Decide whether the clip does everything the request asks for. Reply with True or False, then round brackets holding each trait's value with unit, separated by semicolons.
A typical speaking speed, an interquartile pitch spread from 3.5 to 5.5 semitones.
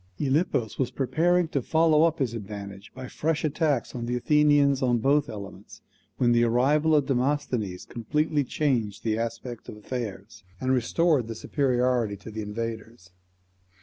True (150 wpm; 4.7 semitones)